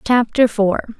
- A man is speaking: No, female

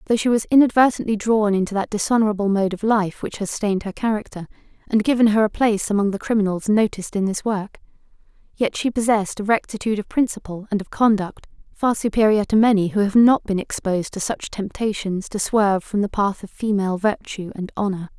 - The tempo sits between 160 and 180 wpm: No, average, 200 wpm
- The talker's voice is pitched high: Yes, high, 205 Hz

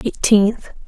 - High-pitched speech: Yes, high, 210 Hz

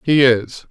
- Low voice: Yes, low, 130 Hz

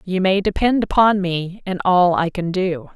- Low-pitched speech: No, medium, 185 Hz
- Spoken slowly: No, fast, 205 wpm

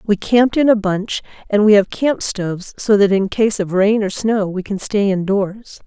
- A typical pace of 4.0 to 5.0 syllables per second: Yes, 4.6 syllables/s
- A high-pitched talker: Yes, high, 205 Hz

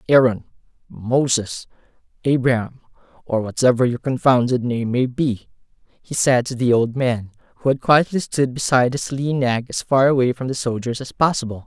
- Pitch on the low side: Yes, low, 125 Hz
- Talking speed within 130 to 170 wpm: Yes, average, 165 wpm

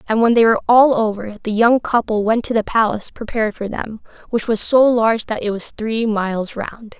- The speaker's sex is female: Yes, female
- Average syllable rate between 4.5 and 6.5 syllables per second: Yes, 5.5 syllables/s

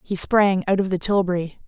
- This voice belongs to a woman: Yes, female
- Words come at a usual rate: No, fast, 215 wpm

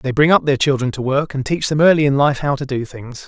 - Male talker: Yes, male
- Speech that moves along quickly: Yes, fast, 310 wpm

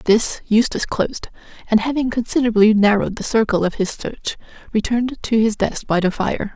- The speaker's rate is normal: Yes, average, 175 wpm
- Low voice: No, high, 220 Hz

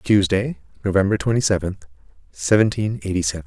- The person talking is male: Yes, male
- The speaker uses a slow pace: Yes, slow, 120 wpm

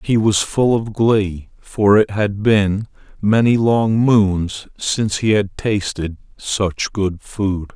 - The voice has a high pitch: No, low, 105 Hz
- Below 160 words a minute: Yes, average, 145 wpm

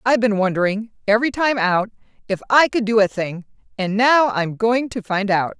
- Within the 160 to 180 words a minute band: No, fast, 205 wpm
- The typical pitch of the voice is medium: No, high, 215 Hz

